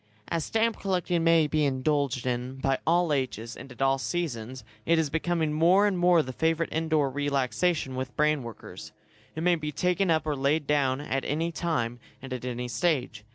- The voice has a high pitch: No, medium, 150 Hz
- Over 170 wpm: Yes, average, 190 wpm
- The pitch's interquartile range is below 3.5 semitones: No, average, 4.1 semitones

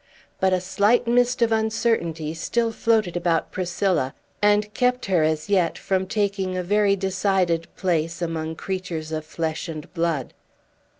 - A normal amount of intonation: Yes, average, 4.0 semitones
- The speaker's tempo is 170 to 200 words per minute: No, average, 145 wpm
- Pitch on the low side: No, medium, 185 Hz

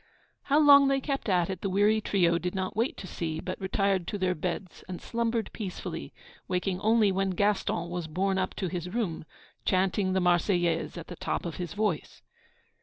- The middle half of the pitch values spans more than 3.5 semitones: No, average, 2.9 semitones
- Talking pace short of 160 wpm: No, average, 190 wpm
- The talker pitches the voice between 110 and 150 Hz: No, medium, 185 Hz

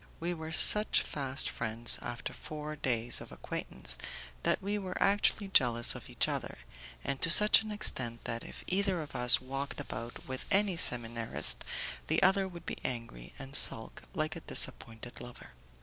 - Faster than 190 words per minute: No, average, 165 wpm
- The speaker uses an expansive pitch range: Yes, wide, 7.5 semitones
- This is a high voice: No, low, 135 Hz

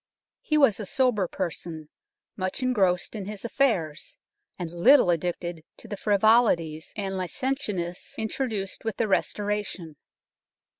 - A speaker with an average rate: No, slow, 120 wpm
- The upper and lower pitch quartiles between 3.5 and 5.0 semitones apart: Yes, average, 4.4 semitones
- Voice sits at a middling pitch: No, high, 195 Hz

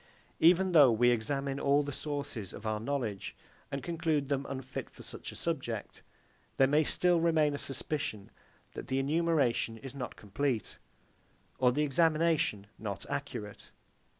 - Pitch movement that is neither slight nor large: Yes, average, 4.2 semitones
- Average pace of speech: Yes, average, 150 wpm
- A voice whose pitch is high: No, medium, 140 Hz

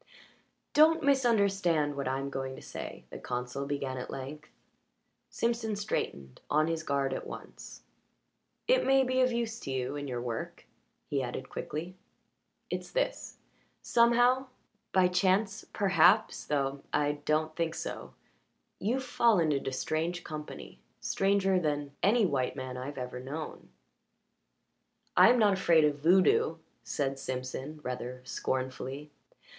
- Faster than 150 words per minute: No, slow, 135 wpm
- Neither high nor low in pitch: Yes, medium, 155 Hz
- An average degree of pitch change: No, wide, 7.0 semitones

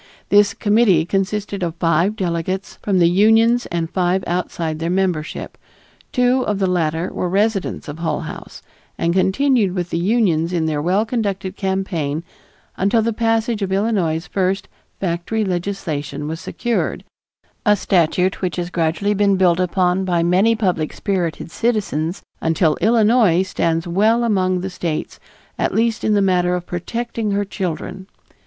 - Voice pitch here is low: No, medium, 185 Hz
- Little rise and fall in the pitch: No, average, 3.4 semitones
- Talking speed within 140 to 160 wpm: Yes, average, 150 wpm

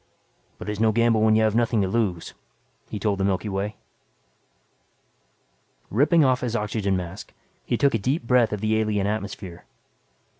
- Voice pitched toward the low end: Yes, low, 110 Hz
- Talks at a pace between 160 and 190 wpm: Yes, average, 165 wpm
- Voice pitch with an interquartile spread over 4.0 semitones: No, average, 2.8 semitones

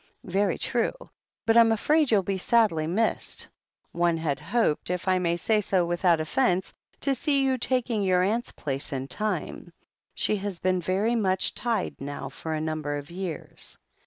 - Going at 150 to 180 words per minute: Yes, average, 170 wpm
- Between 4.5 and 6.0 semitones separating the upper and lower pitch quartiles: Yes, average, 5.2 semitones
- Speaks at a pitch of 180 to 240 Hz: Yes, medium, 185 Hz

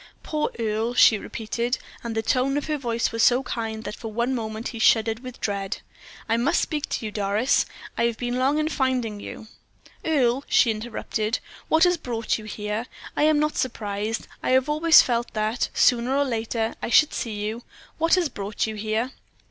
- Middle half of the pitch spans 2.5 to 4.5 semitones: Yes, average, 3.1 semitones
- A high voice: Yes, high, 235 Hz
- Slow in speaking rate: No, average, 195 wpm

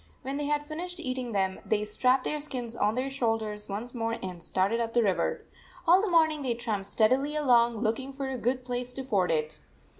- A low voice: No, high, 245 Hz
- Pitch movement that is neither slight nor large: Yes, average, 4.0 semitones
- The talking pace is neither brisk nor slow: No, fast, 215 wpm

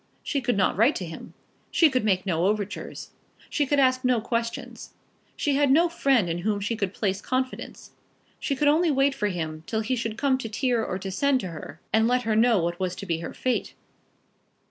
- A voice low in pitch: No, high, 225 Hz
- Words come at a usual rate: No, fast, 210 wpm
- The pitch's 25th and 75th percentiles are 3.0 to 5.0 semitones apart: No, wide, 5.5 semitones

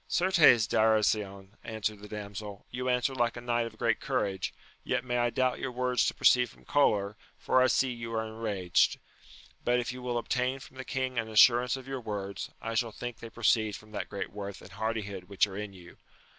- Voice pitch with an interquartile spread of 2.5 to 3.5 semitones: Yes, average, 3.1 semitones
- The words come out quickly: Yes, fast, 210 wpm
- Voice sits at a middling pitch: No, low, 115 Hz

